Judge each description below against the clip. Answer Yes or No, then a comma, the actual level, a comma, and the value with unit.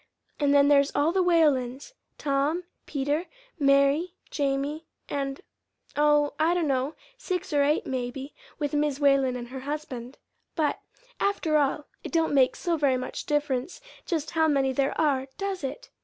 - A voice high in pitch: Yes, very high, 290 Hz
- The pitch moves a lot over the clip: No, narrow, 2.5 semitones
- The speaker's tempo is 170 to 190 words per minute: No, average, 155 wpm